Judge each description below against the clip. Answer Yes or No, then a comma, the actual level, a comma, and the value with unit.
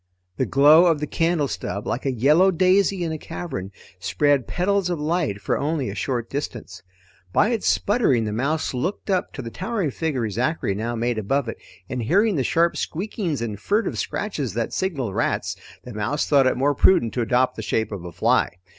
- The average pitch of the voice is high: No, medium, 140 Hz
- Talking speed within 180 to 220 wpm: Yes, average, 200 wpm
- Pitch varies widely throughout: Yes, wide, 6.7 semitones